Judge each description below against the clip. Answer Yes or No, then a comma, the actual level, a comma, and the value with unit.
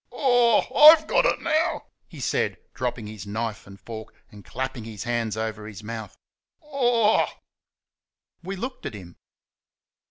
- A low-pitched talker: Yes, low, 115 Hz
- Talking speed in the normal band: Yes, average, 150 wpm